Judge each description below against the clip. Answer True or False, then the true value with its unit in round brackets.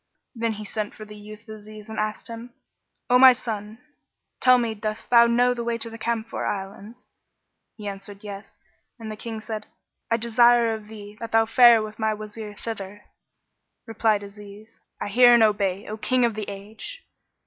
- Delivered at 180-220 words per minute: True (185 wpm)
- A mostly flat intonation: True (1.9 semitones)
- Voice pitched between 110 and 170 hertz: False (220 Hz)